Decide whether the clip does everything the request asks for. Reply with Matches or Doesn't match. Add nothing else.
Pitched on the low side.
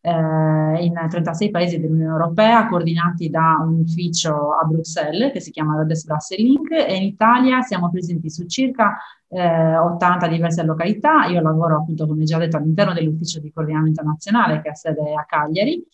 Doesn't match